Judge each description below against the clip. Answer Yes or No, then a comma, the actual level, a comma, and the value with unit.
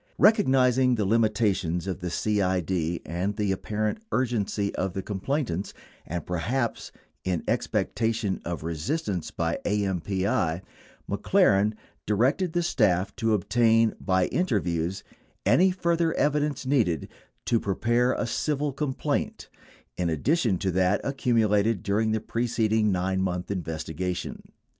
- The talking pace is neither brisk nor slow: No, slow, 130 wpm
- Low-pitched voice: Yes, low, 105 Hz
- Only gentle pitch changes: No, average, 4.9 semitones